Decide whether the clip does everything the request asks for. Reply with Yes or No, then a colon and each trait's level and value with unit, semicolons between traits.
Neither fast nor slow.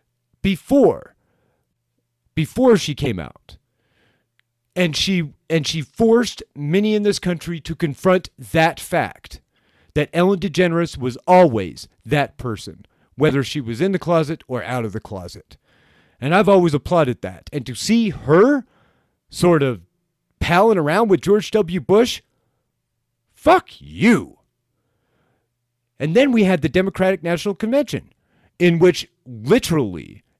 No: slow, 130 wpm